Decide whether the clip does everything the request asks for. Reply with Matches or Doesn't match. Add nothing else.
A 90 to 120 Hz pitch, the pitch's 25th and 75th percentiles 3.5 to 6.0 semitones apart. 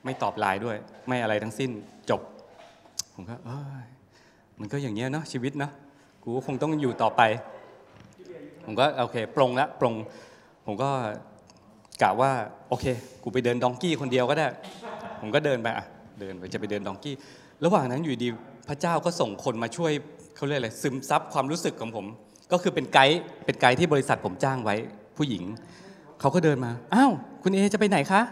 Doesn't match